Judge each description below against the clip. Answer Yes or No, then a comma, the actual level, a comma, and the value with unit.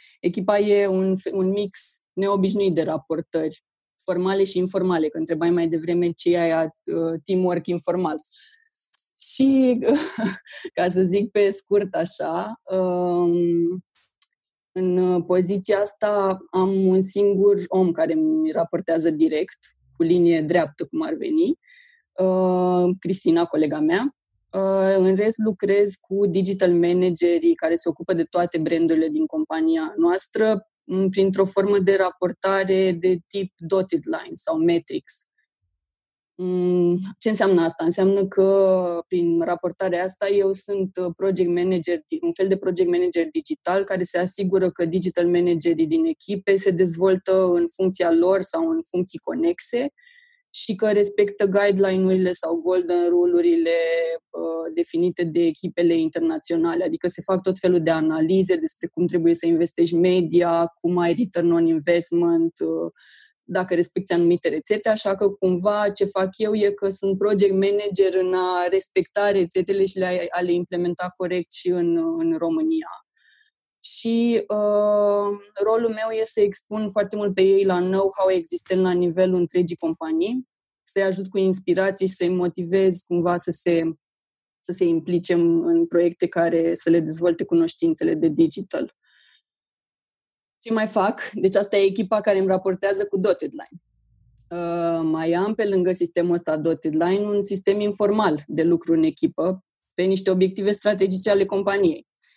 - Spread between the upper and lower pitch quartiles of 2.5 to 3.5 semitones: Yes, average, 2.9 semitones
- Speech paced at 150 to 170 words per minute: No, average, 140 wpm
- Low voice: No, medium, 185 Hz